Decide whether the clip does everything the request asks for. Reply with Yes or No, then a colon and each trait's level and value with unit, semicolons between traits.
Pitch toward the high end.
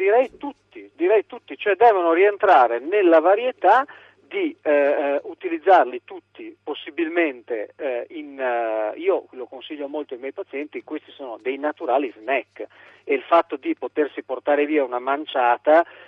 Yes: high, 195 Hz